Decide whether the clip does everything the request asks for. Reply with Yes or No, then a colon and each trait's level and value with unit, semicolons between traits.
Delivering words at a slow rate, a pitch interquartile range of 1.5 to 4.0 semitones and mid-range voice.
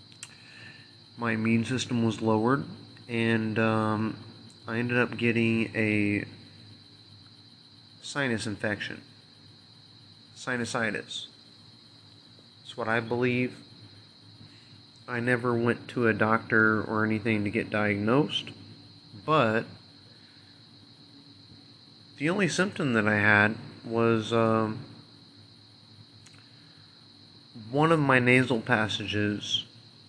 No: slow, 90 wpm; narrow, 2.5 semitones; low, 115 Hz